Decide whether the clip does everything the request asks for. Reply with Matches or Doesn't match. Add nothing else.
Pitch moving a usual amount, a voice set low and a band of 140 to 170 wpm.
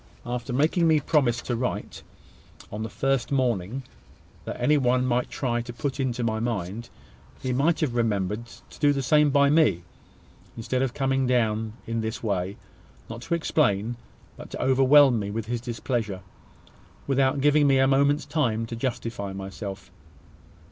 Matches